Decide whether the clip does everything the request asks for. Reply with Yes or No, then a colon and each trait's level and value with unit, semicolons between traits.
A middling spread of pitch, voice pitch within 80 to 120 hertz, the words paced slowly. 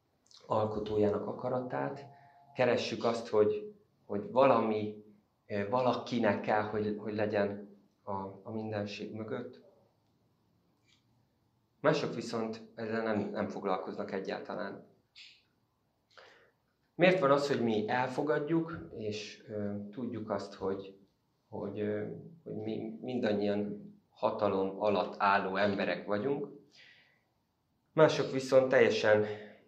Yes: average, 3.0 semitones; low, 105 Hz; slow, 95 wpm